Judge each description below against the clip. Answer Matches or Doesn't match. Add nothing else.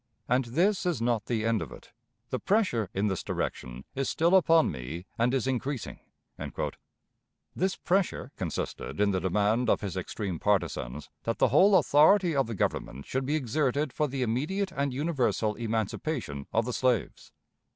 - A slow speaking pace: Doesn't match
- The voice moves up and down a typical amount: Doesn't match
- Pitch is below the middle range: Matches